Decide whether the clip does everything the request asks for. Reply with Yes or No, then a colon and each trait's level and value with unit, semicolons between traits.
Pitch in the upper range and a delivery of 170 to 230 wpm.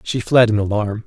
No: low, 110 Hz; fast, 225 wpm